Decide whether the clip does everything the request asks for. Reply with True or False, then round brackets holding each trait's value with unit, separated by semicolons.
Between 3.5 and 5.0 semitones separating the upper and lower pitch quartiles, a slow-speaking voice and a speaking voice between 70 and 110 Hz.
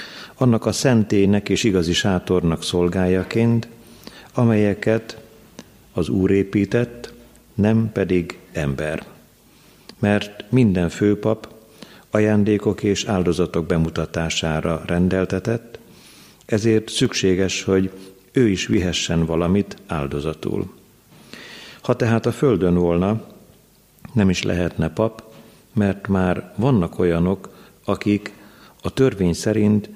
True (3.8 semitones; 95 wpm; 100 Hz)